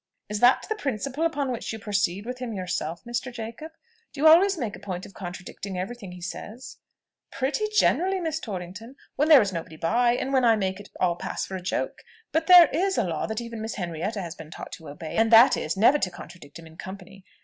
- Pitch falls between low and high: No, high, 220 Hz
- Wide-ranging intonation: Yes, wide, 6.5 semitones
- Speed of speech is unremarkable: No, fast, 225 wpm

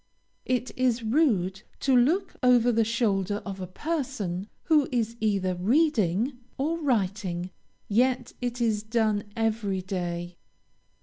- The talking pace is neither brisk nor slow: No, slow, 125 wpm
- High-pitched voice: Yes, high, 225 Hz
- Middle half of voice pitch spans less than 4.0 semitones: No, average, 4.7 semitones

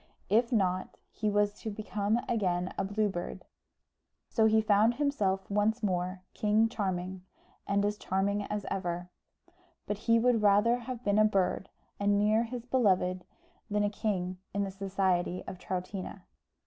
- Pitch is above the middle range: Yes, high, 205 Hz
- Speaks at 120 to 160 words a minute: Yes, average, 155 wpm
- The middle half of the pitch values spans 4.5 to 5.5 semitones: No, narrow, 2.5 semitones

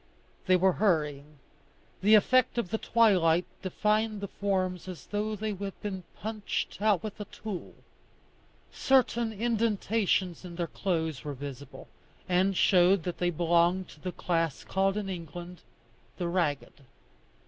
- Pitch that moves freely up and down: No, average, 3.5 semitones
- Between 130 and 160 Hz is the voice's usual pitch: No, medium, 185 Hz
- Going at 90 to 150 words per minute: Yes, average, 140 wpm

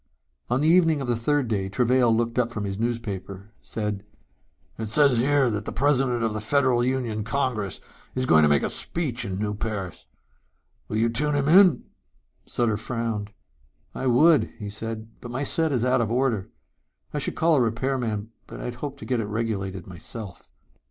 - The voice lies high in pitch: No, low, 115 Hz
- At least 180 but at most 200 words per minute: Yes, average, 190 wpm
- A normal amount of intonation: Yes, average, 3.8 semitones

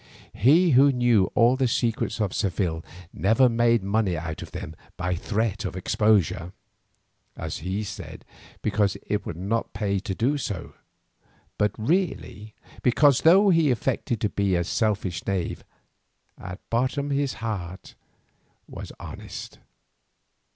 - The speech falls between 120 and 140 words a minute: Yes, slow, 135 wpm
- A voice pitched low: Yes, low, 110 Hz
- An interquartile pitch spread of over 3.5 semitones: Yes, average, 4.7 semitones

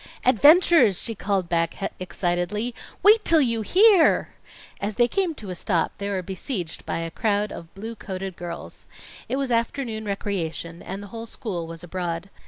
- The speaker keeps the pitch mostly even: No, average, 4.9 semitones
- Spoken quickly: No, average, 170 wpm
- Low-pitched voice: No, high, 200 Hz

